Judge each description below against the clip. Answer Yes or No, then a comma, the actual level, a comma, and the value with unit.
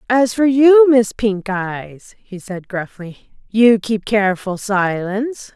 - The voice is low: No, high, 215 Hz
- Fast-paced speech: No, average, 140 wpm